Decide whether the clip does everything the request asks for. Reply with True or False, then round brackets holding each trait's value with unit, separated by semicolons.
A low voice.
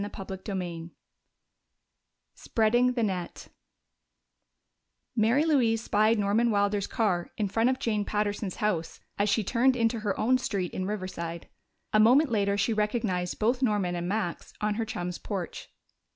False (210 Hz)